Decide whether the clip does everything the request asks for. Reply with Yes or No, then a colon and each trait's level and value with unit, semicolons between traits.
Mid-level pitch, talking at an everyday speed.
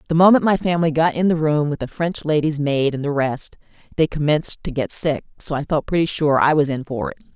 No: medium, 155 Hz; fast, 255 wpm